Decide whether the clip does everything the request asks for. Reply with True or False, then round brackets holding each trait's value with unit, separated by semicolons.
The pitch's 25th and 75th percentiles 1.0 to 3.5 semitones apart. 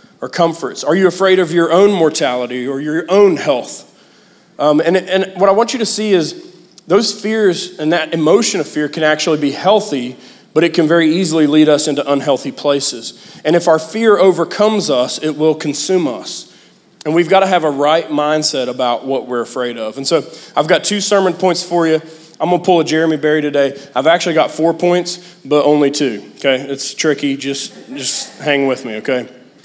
False (4.2 semitones)